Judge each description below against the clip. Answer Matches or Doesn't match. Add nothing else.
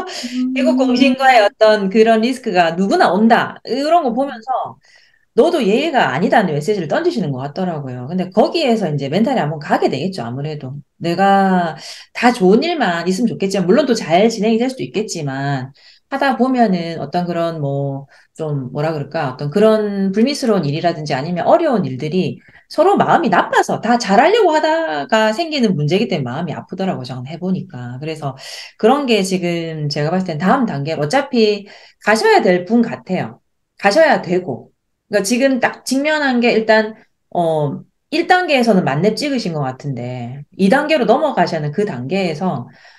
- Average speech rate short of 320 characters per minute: Doesn't match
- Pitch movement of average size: Doesn't match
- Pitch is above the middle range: Matches